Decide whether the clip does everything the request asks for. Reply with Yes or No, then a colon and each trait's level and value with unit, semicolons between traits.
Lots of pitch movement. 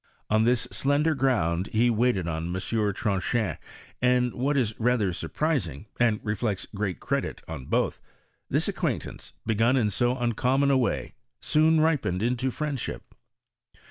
No: average, 4.6 semitones